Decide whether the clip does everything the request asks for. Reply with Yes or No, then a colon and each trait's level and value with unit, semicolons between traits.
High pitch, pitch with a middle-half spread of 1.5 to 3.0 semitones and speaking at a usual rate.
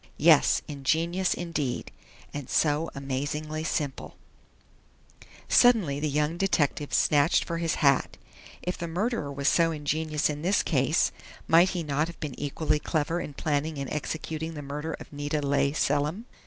No: medium, 150 Hz; narrow, 2.4 semitones; average, 150 wpm